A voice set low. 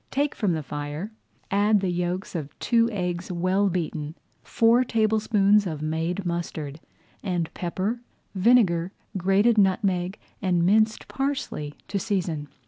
No: medium, 185 Hz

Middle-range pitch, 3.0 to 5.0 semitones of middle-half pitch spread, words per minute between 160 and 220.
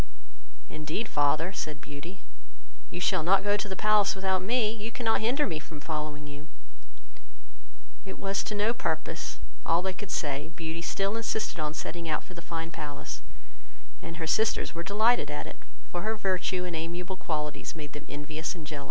Yes: medium, 170 Hz; average, 4.5 semitones; average, 180 wpm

